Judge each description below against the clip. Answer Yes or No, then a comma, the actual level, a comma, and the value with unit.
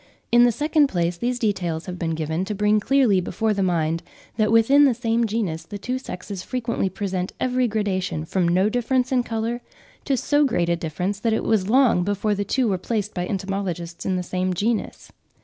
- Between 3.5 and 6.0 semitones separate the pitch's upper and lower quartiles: Yes, average, 4.6 semitones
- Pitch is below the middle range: No, high, 205 Hz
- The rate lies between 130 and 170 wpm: No, average, 200 wpm